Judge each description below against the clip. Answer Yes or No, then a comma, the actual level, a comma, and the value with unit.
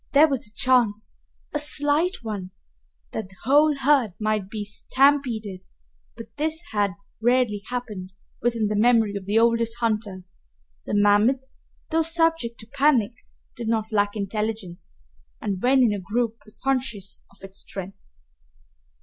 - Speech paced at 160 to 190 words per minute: No, average, 145 wpm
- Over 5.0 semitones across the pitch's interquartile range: No, average, 4.1 semitones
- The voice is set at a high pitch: Yes, high, 225 Hz